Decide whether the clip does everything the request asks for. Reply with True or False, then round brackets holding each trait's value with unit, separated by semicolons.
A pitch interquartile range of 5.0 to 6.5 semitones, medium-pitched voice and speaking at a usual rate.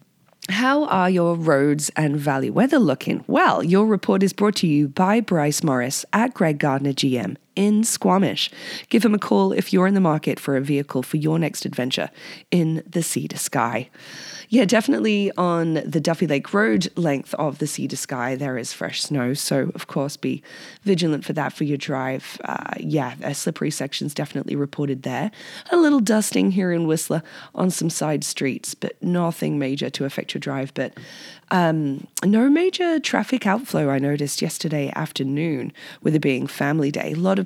True (5.6 semitones; 165 Hz; 185 wpm)